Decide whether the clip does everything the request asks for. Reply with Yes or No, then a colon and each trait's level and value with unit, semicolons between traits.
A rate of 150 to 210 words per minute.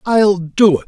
Yes: fast, 205 wpm